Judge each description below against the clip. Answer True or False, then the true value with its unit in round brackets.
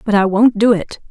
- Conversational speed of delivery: False (270 wpm)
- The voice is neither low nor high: False (210 Hz)